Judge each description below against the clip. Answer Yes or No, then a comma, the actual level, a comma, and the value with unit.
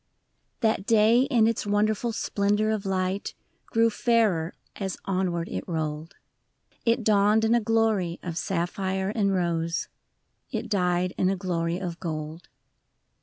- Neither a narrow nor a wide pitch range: Yes, average, 3.8 semitones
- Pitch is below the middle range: No, high, 195 Hz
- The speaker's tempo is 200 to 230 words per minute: No, average, 140 wpm